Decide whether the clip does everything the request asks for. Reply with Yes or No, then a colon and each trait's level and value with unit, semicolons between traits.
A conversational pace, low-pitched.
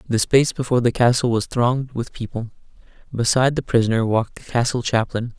Yes: average, 180 wpm; low, 120 Hz